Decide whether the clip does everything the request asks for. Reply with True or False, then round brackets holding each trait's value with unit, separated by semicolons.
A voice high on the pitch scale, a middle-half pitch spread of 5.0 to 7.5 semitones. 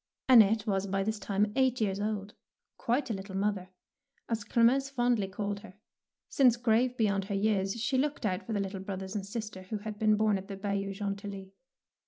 False (205 Hz; 2.6 semitones)